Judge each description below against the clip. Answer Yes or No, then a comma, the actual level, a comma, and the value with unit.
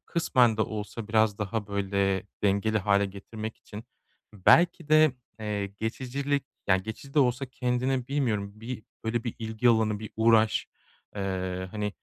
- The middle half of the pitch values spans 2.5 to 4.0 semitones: Yes, average, 3.4 semitones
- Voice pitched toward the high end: No, low, 110 Hz